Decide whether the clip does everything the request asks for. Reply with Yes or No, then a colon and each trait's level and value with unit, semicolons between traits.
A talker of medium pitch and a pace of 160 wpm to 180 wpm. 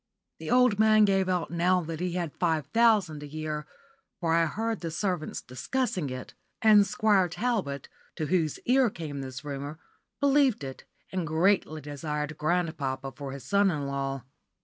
Yes: medium, 165 Hz; average, 165 wpm